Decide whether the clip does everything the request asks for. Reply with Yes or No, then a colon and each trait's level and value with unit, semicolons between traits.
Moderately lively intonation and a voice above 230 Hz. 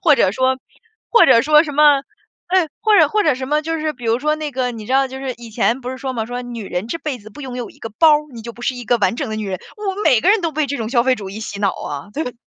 Yes: average, 4.7 semitones; very high, 260 Hz